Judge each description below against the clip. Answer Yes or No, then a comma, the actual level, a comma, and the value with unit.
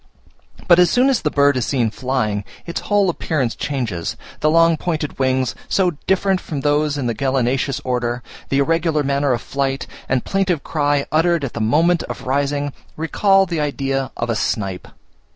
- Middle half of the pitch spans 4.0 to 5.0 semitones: Yes, average, 4.3 semitones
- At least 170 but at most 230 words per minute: Yes, average, 175 wpm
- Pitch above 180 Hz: No, medium, 140 Hz